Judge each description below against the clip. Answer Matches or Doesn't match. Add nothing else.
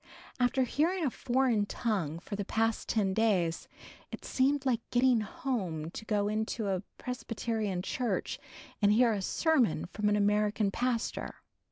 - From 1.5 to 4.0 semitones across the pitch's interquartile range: Matches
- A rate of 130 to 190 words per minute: Matches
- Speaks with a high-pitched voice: Matches